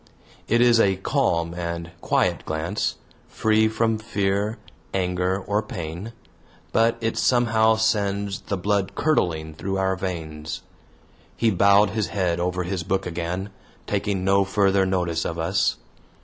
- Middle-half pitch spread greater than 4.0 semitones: No, average, 3.4 semitones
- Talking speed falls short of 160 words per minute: Yes, slow, 135 wpm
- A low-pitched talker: Yes, very low, 95 Hz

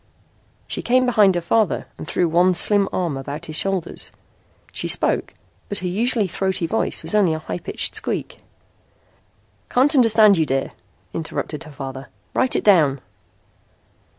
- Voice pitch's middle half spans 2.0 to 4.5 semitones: No, average, 5.1 semitones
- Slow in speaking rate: No, average, 150 wpm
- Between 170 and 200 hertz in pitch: Yes, medium, 185 Hz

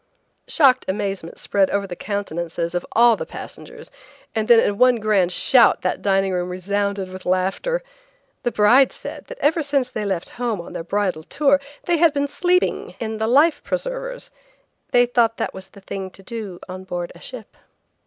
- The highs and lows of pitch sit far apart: Yes, wide, 5.8 semitones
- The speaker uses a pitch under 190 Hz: No, high, 210 Hz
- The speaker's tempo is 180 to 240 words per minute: Yes, average, 185 wpm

